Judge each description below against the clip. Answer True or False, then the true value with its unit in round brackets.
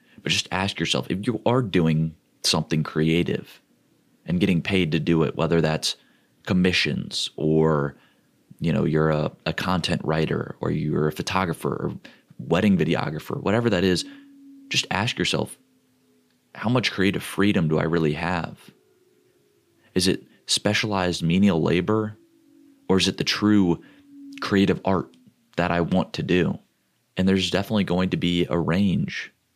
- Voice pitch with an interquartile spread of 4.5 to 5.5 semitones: False (3.9 semitones)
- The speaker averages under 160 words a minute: True (145 wpm)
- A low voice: True (90 Hz)